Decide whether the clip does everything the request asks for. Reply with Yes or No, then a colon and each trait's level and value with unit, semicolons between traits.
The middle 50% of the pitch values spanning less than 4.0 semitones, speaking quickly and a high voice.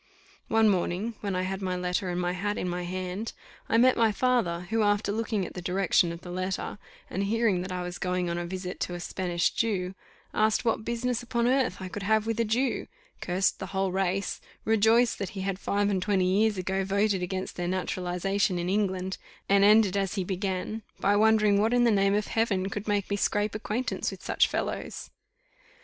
Yes: average, 2.9 semitones; fast, 210 wpm; high, 195 Hz